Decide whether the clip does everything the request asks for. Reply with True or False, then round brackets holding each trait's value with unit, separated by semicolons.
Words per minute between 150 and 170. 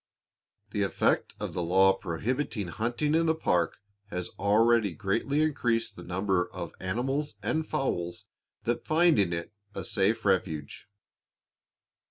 False (135 wpm)